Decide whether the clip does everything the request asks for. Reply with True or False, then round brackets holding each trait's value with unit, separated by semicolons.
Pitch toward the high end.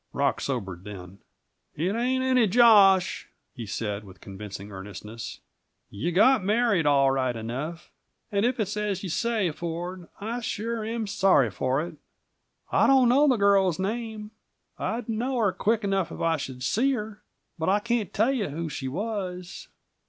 True (195 Hz)